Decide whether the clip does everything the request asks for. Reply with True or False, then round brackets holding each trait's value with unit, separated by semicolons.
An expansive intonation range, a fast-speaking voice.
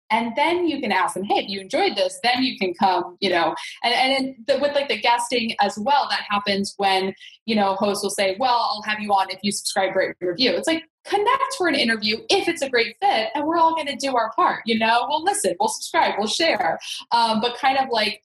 True (6.8 semitones; 250 wpm)